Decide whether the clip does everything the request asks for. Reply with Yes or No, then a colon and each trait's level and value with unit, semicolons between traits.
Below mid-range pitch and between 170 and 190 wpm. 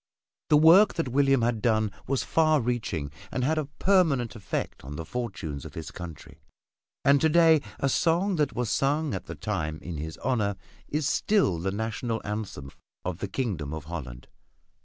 Yes: low, 120 Hz; average, 180 wpm